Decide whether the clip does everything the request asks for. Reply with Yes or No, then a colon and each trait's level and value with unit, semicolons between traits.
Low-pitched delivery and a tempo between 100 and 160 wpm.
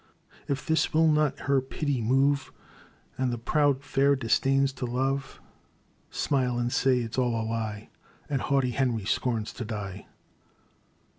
Yes: low, 130 Hz; average, 155 wpm